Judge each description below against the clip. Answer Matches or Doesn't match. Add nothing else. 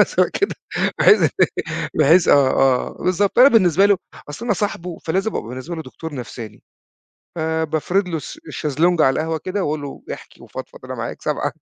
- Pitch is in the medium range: Matches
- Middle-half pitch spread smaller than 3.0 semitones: Doesn't match